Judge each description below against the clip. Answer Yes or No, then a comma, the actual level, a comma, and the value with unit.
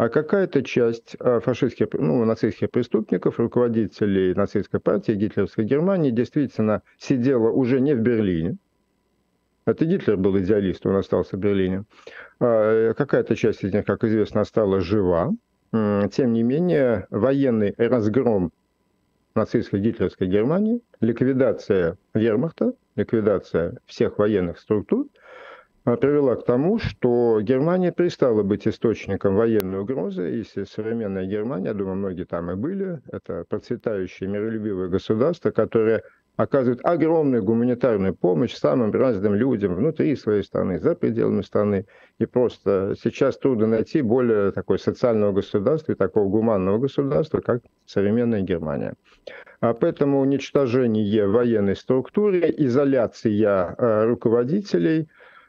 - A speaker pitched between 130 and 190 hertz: No, low, 115 Hz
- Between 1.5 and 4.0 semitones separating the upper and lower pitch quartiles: No, average, 4.4 semitones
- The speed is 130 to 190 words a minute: No, average, 115 wpm